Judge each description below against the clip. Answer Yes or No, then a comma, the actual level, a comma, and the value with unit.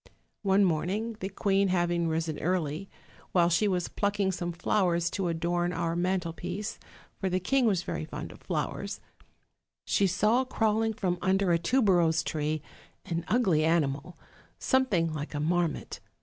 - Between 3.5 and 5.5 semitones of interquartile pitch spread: No, average, 3.0 semitones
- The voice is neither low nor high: Yes, medium, 180 Hz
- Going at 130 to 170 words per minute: Yes, average, 150 wpm